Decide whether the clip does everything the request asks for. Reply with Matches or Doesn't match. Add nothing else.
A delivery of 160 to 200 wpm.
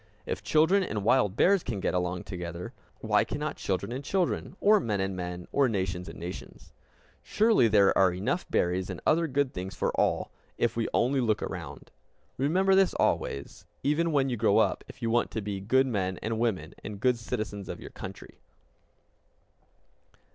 Matches